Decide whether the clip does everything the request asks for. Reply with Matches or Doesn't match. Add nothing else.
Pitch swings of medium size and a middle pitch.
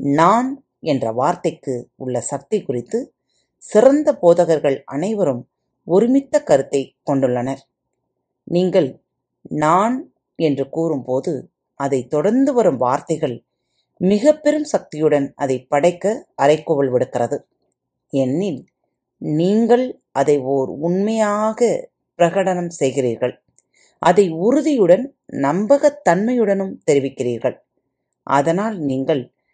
Doesn't match